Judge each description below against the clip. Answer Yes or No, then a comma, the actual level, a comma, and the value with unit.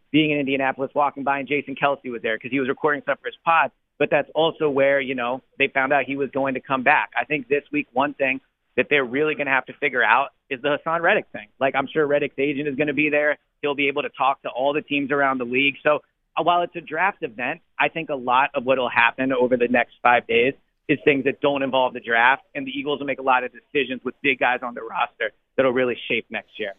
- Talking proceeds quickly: Yes, fast, 270 wpm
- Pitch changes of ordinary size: No, narrow, 1.8 semitones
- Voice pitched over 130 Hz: Yes, medium, 140 Hz